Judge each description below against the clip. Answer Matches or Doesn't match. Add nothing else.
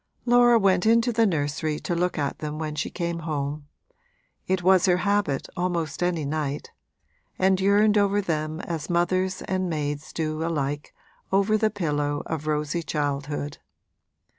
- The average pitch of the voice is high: Doesn't match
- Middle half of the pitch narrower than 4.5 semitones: Matches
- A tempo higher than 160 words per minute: Doesn't match